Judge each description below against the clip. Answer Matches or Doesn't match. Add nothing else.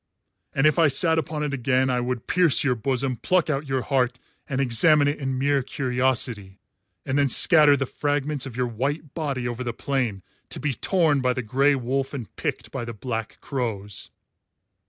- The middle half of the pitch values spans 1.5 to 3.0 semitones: Matches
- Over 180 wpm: Matches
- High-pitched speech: Doesn't match